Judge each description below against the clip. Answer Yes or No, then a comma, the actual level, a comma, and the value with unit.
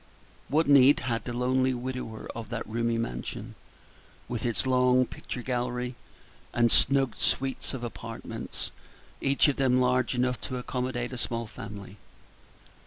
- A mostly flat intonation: Yes, narrow, 1.7 semitones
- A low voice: Yes, low, 125 Hz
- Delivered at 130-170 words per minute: Yes, average, 140 wpm